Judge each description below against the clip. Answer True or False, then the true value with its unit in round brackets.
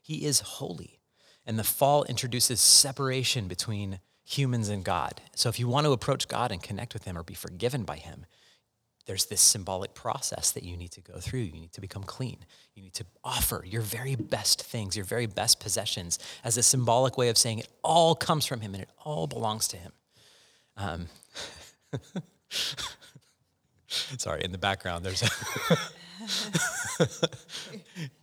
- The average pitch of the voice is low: True (115 Hz)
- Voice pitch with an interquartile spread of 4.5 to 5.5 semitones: True (5.1 semitones)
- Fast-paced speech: False (170 wpm)